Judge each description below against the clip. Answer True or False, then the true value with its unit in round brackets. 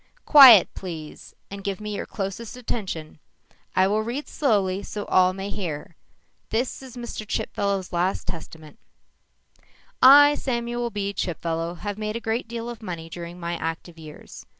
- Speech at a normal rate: True (150 wpm)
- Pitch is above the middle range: True (200 Hz)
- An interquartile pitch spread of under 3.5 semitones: False (5.1 semitones)